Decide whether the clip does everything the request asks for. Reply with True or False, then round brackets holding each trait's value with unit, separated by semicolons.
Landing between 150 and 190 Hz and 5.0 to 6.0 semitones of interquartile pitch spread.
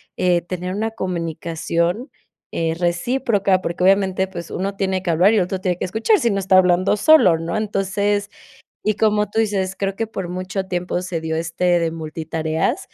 False (185 Hz; 2.8 semitones)